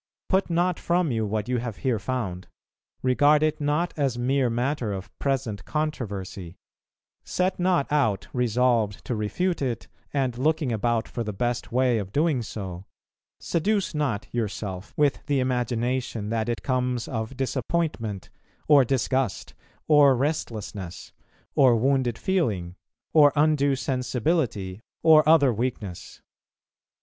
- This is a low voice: Yes, low, 125 Hz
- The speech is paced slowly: Yes, slow, 130 wpm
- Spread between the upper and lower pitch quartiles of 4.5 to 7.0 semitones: Yes, average, 4.8 semitones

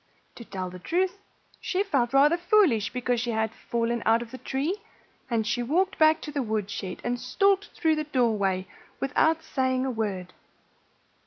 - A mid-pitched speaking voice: No, very high, 250 Hz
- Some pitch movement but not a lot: No, wide, 6.1 semitones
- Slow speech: No, average, 170 wpm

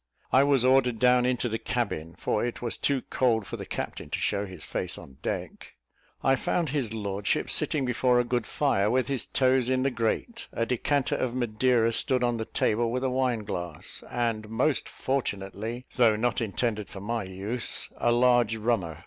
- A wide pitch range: No, average, 2.9 semitones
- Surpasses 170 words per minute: Yes, average, 190 wpm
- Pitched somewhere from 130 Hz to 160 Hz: No, low, 120 Hz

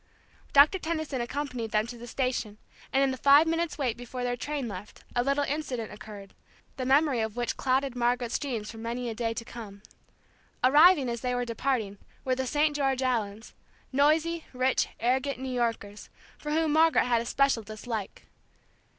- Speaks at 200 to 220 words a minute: No, average, 175 wpm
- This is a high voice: Yes, very high, 250 Hz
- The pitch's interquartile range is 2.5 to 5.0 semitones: Yes, average, 3.5 semitones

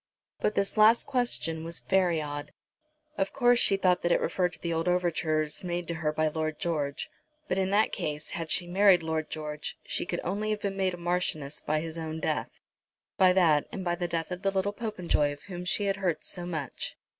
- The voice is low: No, medium, 175 Hz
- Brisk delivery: Yes, fast, 215 wpm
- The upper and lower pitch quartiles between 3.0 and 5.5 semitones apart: Yes, average, 3.4 semitones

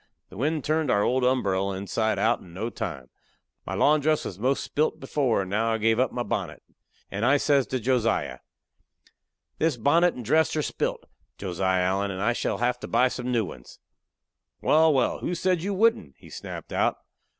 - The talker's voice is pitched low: Yes, low, 125 Hz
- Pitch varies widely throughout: Yes, wide, 6.4 semitones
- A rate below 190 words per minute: No, average, 195 wpm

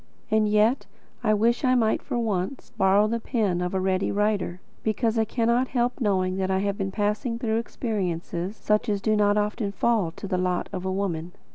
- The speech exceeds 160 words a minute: Yes, fast, 205 wpm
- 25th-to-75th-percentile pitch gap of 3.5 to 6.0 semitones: No, average, 3.1 semitones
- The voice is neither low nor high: No, high, 210 Hz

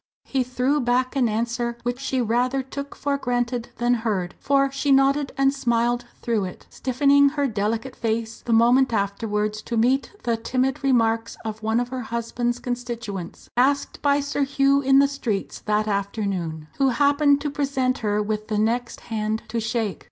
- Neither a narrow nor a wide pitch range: Yes, average, 3.5 semitones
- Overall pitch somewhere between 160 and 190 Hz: No, high, 245 Hz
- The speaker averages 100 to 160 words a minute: No, average, 175 wpm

